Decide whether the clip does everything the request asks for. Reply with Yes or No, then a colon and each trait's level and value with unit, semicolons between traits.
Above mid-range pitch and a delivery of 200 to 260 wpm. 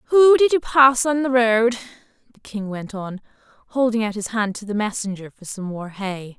Yes: high, 225 Hz; fast, 205 wpm